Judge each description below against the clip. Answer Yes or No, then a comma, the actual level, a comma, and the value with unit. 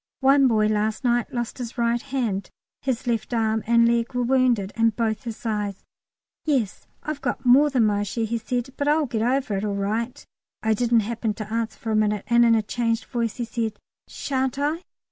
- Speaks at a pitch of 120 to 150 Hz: No, high, 235 Hz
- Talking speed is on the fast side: Yes, fast, 210 wpm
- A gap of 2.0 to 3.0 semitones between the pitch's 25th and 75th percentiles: Yes, narrow, 2.4 semitones